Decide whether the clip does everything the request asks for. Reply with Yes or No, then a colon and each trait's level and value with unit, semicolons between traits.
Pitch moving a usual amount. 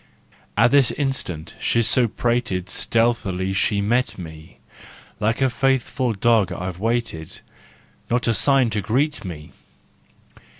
Yes: average, 4.7 semitones